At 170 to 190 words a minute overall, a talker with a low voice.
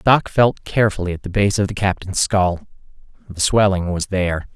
Yes: average, 185 wpm; very low, 95 Hz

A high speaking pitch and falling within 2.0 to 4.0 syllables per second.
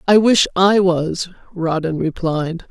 No: medium, 175 Hz; 3.7 syllables/s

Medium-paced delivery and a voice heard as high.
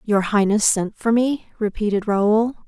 Yes: average, 155 wpm; high, 215 Hz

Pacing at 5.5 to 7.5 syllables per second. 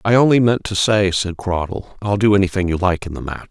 Yes: 6.2 syllables/s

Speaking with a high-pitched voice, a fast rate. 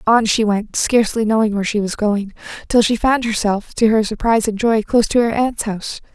Yes: high, 220 Hz; fast, 225 wpm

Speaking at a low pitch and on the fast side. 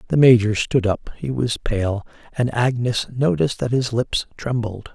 No: low, 120 Hz; average, 170 wpm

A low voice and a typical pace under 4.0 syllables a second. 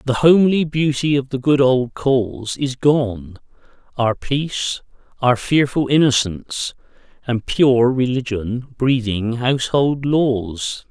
Yes: low, 130 Hz; 3.8 syllables/s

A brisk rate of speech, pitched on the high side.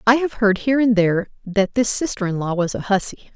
Yes: fast, 250 wpm; high, 210 Hz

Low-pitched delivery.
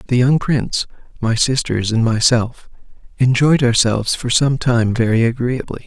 Yes: low, 120 Hz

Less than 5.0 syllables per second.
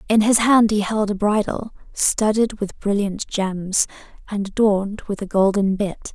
Yes: 4.4 syllables/s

